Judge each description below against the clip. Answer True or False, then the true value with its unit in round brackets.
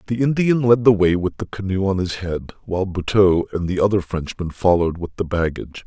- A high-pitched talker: False (95 Hz)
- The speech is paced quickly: True (215 wpm)